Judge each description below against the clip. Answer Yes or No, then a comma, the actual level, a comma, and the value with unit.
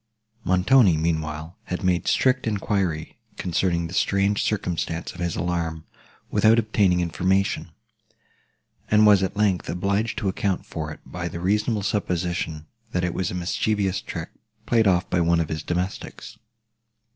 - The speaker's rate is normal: Yes, average, 145 wpm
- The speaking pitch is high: No, very low, 90 Hz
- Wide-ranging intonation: No, average, 3.0 semitones